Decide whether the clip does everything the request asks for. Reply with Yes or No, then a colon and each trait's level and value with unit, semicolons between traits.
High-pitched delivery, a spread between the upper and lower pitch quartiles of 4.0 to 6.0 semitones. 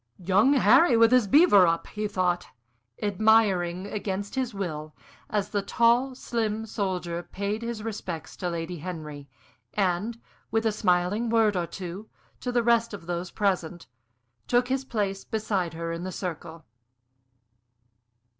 Yes: high, 200 Hz; average, 4.3 semitones